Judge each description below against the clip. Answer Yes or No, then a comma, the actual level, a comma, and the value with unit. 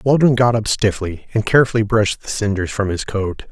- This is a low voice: Yes, low, 105 Hz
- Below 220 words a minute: Yes, fast, 205 wpm